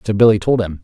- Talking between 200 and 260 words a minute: No, fast, 285 wpm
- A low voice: Yes, low, 105 Hz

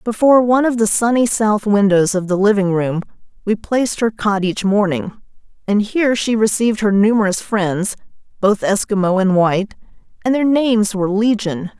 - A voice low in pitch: No, high, 210 Hz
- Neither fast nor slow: Yes, average, 170 wpm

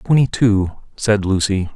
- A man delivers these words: Yes, male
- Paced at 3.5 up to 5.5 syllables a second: Yes, 4.3 syllables/s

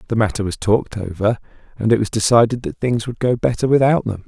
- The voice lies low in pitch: Yes, low, 110 Hz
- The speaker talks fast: Yes, fast, 225 wpm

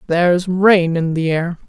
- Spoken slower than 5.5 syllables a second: Yes, 4.2 syllables/s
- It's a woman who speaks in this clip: Yes, female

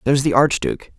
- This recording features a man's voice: Yes, male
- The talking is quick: No, average, 185 wpm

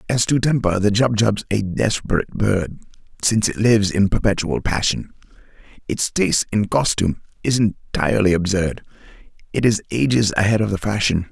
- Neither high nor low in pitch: No, low, 105 Hz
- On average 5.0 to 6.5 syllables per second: Yes, 5.4 syllables/s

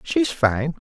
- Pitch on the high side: No, low, 115 Hz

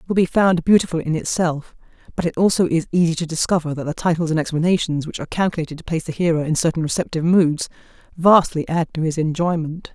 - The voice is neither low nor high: Yes, medium, 165 Hz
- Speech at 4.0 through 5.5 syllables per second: No, 6.5 syllables/s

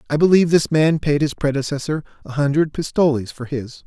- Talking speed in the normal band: Yes, average, 185 wpm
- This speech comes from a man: Yes, male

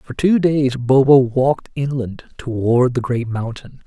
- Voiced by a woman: No, male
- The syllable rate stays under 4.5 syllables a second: Yes, 4.2 syllables/s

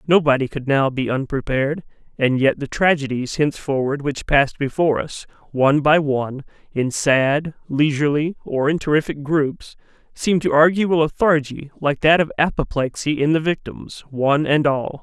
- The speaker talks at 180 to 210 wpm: No, average, 155 wpm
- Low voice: No, medium, 145 Hz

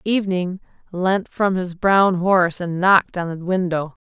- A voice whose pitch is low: No, medium, 185 Hz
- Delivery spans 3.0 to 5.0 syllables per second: Yes, 4.5 syllables/s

